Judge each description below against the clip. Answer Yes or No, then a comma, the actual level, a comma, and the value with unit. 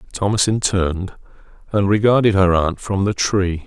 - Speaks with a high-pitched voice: No, low, 100 Hz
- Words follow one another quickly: No, average, 145 wpm